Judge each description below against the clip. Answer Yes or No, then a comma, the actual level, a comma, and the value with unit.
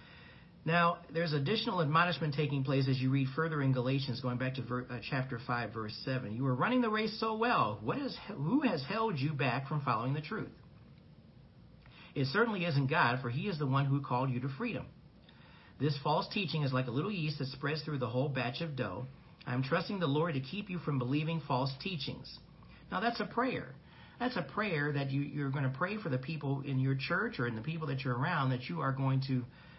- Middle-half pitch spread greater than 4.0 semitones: Yes, average, 4.5 semitones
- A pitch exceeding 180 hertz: No, medium, 140 Hz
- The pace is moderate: No, fast, 225 wpm